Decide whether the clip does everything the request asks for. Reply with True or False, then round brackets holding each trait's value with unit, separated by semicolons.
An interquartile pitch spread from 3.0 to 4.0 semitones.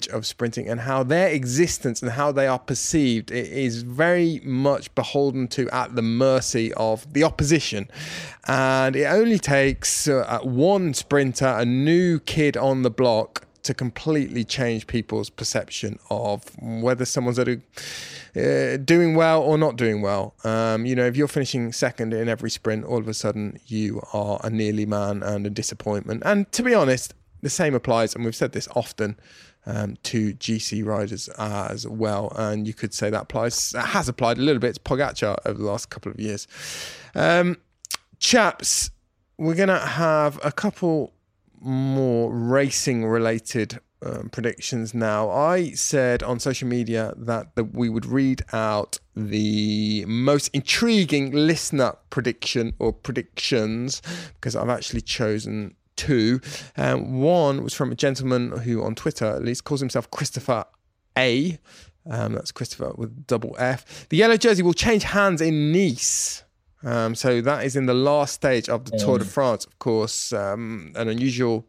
False (4.4 semitones)